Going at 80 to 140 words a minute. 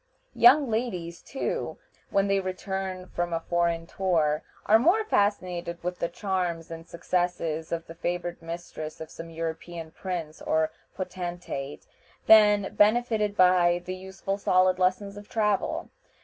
Yes: slow, 135 wpm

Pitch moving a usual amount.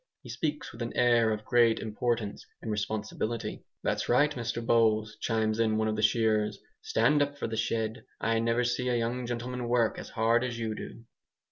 No: narrow, 1.9 semitones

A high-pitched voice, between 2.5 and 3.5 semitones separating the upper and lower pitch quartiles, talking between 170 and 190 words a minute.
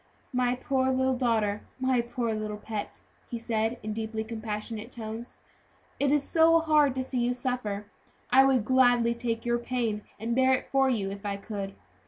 Yes: high, 235 Hz; average, 3.0 semitones; average, 185 wpm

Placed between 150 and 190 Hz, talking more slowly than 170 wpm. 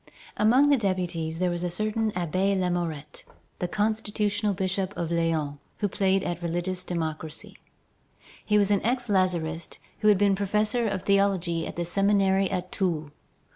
Yes: medium, 185 Hz; average, 155 wpm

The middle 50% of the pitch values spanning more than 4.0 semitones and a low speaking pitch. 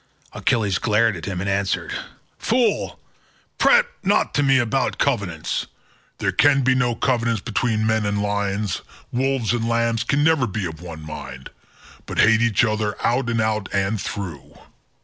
No: average, 3.6 semitones; low, 110 Hz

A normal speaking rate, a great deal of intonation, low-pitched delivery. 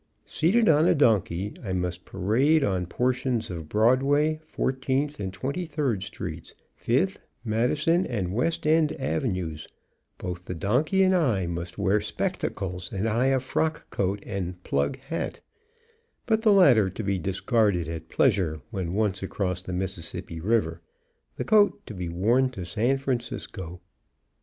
Yes: average, 145 wpm; wide, 6.9 semitones; low, 110 Hz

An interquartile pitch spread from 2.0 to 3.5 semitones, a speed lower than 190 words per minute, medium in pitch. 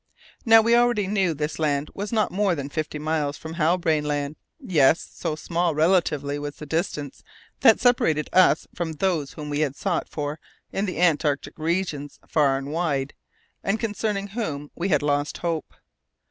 No: average, 4.4 semitones; average, 170 wpm; medium, 160 Hz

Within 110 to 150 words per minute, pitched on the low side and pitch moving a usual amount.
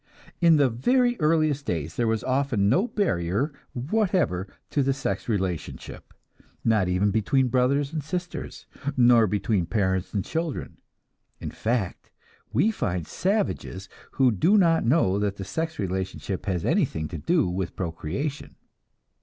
No: average, 140 wpm; low, 125 Hz; wide, 8.5 semitones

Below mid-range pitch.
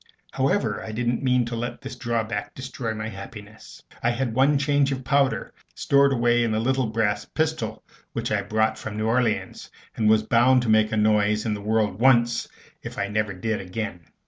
Yes: low, 115 Hz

